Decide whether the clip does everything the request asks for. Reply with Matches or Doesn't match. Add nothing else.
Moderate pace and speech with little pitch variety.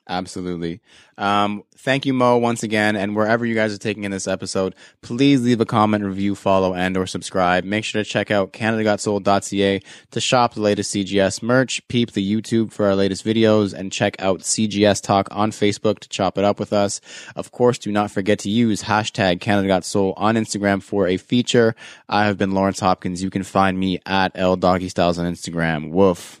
Matches